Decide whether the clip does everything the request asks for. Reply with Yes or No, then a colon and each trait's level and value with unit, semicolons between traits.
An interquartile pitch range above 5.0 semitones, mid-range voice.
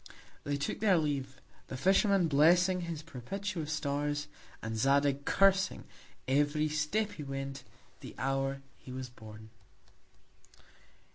No: average, 4.1 semitones; medium, 145 Hz